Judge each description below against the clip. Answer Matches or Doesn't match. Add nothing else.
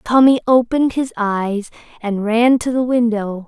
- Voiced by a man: Doesn't match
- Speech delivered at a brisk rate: Doesn't match